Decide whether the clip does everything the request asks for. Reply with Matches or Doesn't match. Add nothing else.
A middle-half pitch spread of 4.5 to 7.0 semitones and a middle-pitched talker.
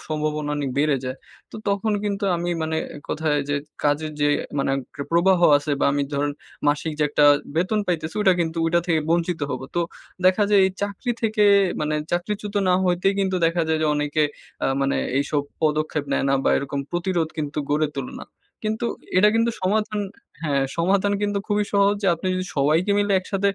Matches